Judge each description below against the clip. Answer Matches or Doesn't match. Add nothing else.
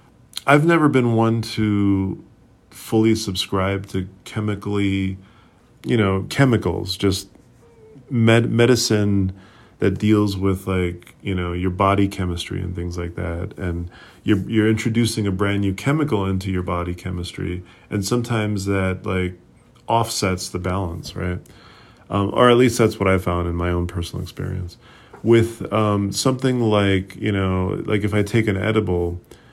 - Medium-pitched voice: Doesn't match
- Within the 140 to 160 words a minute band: Matches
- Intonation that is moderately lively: Matches